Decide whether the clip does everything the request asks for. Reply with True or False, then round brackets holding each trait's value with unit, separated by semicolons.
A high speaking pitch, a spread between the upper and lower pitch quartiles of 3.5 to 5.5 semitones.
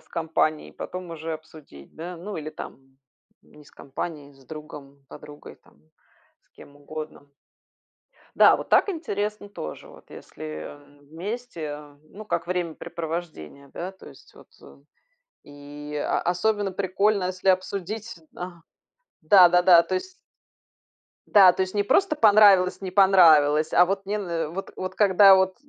False (175 Hz; 4.2 semitones)